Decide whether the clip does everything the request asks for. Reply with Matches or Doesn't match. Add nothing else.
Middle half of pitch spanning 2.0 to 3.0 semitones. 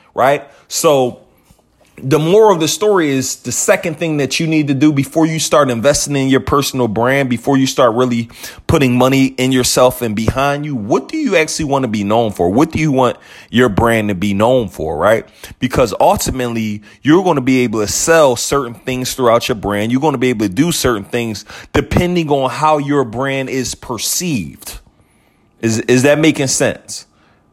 Doesn't match